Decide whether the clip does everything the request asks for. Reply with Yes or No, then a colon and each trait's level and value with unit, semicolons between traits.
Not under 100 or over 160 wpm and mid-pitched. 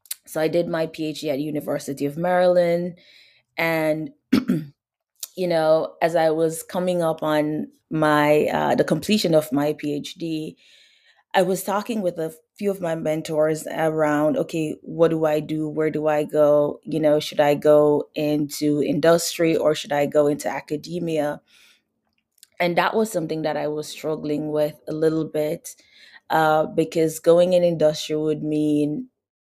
Yes: average, 155 wpm; medium, 155 Hz